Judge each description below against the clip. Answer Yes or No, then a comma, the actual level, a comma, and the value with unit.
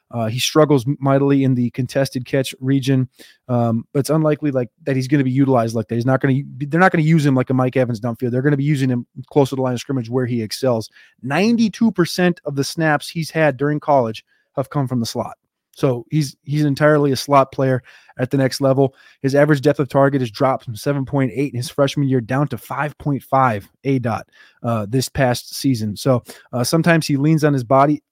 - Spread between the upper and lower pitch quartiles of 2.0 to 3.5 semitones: Yes, narrow, 2.5 semitones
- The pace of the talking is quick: Yes, fast, 235 wpm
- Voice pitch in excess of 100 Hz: Yes, low, 135 Hz